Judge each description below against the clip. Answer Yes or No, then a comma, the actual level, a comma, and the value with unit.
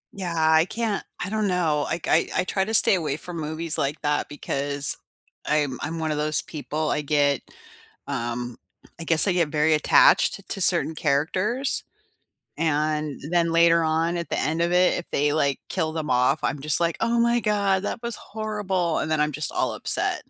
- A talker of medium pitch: Yes, medium, 160 Hz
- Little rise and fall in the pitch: No, average, 3.5 semitones